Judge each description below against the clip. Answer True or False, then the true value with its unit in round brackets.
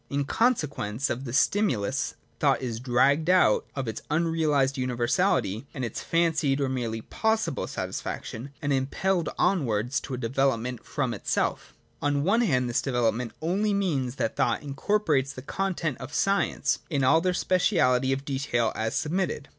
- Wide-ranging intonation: False (4.9 semitones)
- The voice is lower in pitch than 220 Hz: True (135 Hz)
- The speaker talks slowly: False (155 wpm)